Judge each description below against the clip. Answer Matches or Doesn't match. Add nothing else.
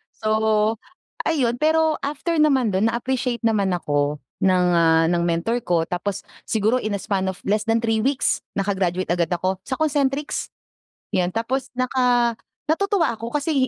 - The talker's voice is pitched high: Matches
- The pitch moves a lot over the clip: Matches